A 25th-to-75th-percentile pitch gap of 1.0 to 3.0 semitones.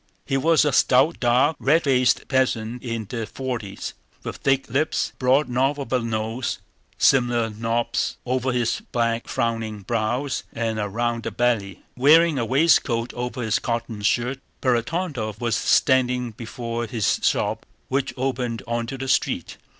Yes: narrow, 2.4 semitones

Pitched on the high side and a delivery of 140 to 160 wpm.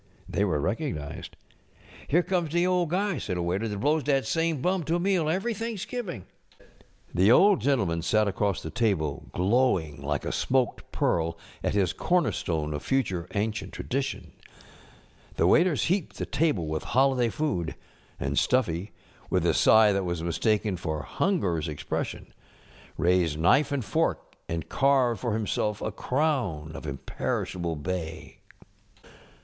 No: low, 110 Hz; average, 155 wpm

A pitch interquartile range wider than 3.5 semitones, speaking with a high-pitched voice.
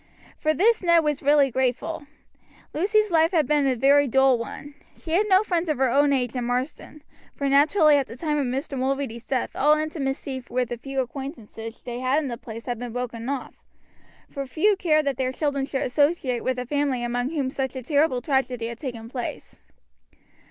No: average, 3.2 semitones; very high, 270 Hz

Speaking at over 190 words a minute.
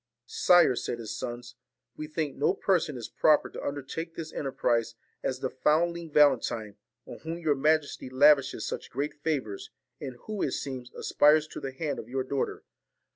No: average, 180 wpm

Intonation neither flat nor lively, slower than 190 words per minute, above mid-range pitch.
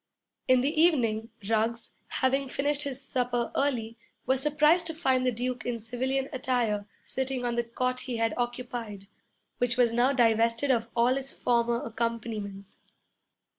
No: narrow, 2.3 semitones; average, 150 wpm; high, 245 Hz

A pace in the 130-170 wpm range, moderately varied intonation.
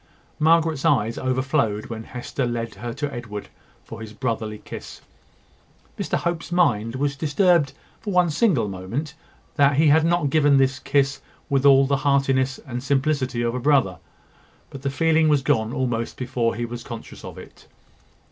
Yes: average, 165 wpm; average, 3.7 semitones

